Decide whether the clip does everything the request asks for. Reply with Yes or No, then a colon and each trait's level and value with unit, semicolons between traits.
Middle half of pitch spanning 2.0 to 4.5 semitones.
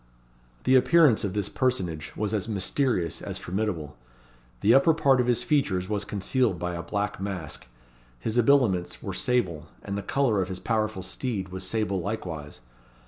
No: average, 5.1 semitones